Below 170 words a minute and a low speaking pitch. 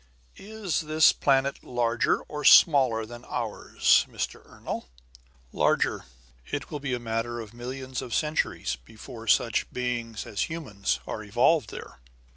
Yes: slow, 135 wpm; low, 120 Hz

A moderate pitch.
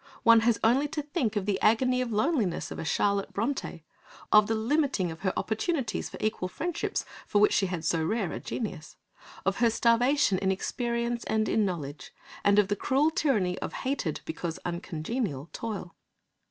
No: high, 220 Hz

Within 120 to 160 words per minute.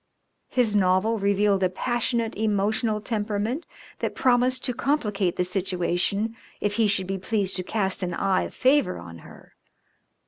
Yes: average, 150 wpm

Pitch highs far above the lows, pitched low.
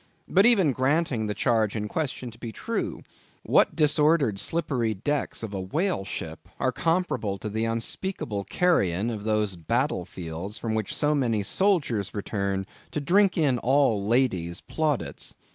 Yes: wide, 6.6 semitones; low, 115 Hz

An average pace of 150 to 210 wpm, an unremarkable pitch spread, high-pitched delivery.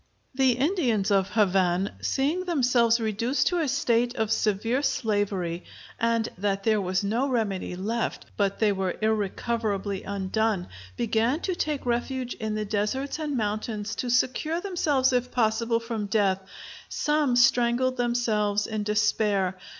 No: average, 140 wpm; average, 3.6 semitones; high, 225 Hz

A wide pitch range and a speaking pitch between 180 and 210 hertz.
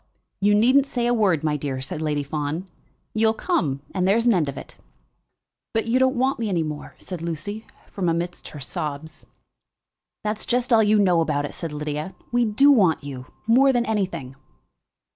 Yes: wide, 7.1 semitones; medium, 185 Hz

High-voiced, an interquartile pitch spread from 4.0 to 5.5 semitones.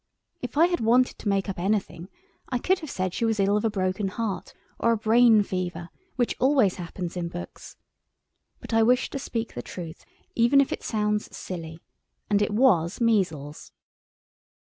Yes: high, 210 Hz; average, 4.3 semitones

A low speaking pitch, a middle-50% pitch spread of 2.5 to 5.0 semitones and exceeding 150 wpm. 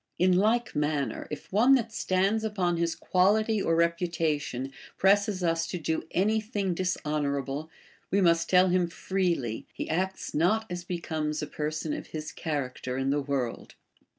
No: medium, 170 Hz; average, 4.1 semitones; average, 160 wpm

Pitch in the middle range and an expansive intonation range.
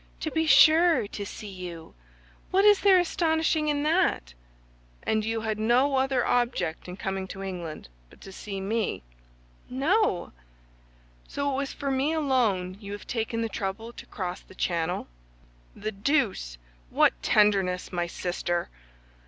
No: high, 220 Hz; wide, 7.2 semitones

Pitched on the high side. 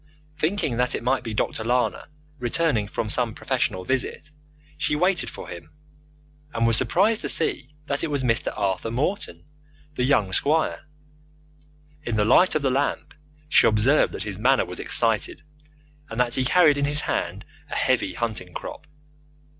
No: low, 125 Hz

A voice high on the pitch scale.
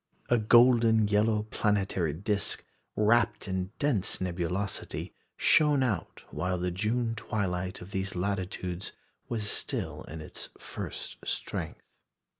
No: low, 100 Hz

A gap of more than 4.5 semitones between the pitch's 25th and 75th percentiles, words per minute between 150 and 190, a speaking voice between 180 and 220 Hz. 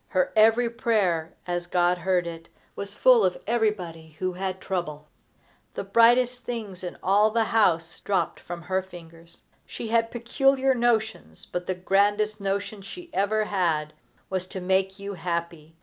No: average, 4.0 semitones; average, 155 wpm; high, 190 Hz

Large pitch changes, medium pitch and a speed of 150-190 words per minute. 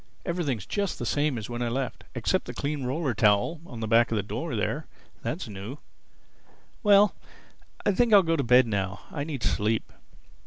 No: wide, 6.6 semitones; low, 130 Hz; average, 170 wpm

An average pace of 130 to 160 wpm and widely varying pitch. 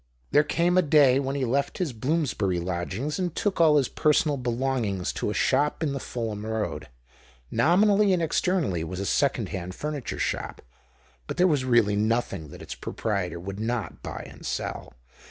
No: average, 180 wpm; wide, 6.8 semitones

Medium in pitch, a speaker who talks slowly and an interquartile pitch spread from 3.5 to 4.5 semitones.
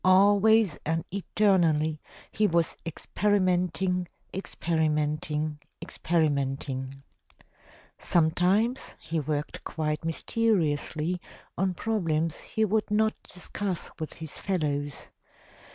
Yes: medium, 170 Hz; slow, 85 wpm; average, 4.2 semitones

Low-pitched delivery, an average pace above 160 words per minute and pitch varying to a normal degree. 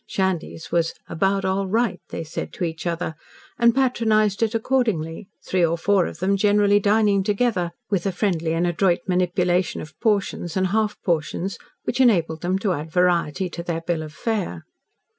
No: medium, 185 Hz; average, 175 wpm; average, 3.4 semitones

